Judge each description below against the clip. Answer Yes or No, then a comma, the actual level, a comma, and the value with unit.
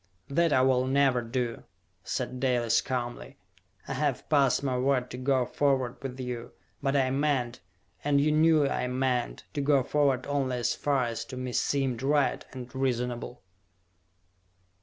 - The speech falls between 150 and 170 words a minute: Yes, average, 160 wpm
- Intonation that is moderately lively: No, narrow, 2.0 semitones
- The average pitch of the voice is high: No, low, 130 Hz